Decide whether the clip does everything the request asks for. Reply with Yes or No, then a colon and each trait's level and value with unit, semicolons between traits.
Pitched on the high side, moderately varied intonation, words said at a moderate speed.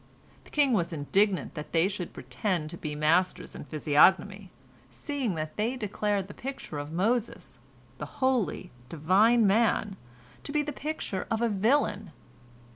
No: high, 200 Hz; wide, 5.8 semitones; average, 150 wpm